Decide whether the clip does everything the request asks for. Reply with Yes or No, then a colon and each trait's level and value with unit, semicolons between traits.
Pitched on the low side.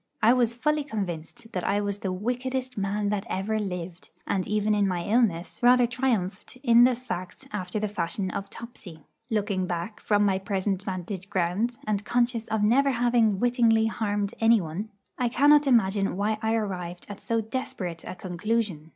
No: high, 210 Hz